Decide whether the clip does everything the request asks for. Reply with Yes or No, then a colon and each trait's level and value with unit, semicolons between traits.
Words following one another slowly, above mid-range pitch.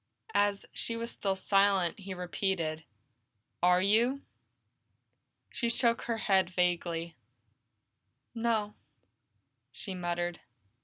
Yes: slow, 95 wpm; high, 195 Hz